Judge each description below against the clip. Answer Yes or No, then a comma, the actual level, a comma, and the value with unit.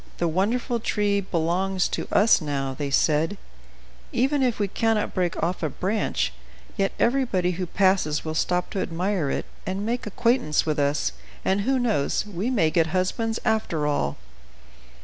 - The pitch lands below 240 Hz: Yes, high, 190 Hz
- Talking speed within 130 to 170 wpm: Yes, average, 160 wpm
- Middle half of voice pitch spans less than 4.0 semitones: No, average, 5.3 semitones